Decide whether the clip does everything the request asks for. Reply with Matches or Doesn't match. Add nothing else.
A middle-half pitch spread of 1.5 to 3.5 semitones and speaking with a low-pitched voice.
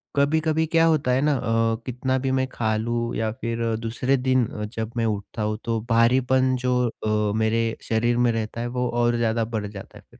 Matches